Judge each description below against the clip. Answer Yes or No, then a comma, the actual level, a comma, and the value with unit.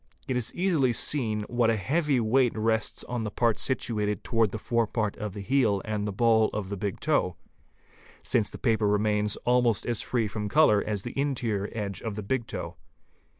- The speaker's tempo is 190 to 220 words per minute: Yes, average, 195 wpm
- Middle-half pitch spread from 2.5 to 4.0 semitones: Yes, average, 2.8 semitones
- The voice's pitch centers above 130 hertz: No, low, 110 Hz